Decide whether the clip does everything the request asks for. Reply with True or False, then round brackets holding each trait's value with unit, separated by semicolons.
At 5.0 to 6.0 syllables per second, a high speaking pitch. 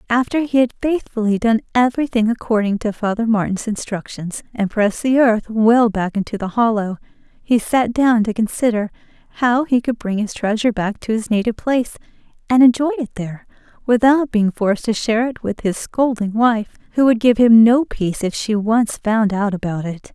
True (5.3 syllables/s; 225 Hz)